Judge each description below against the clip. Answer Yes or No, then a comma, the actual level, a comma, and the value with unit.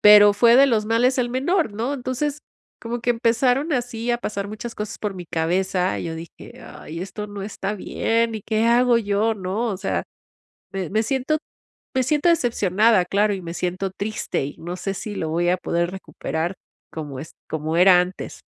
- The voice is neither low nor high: No, high, 210 Hz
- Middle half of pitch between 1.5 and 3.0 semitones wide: No, average, 4.6 semitones